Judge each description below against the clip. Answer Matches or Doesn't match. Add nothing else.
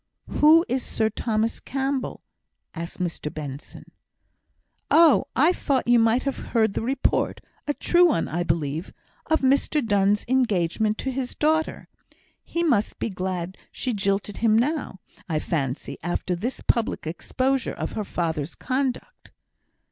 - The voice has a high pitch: Matches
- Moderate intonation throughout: Doesn't match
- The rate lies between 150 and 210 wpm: Doesn't match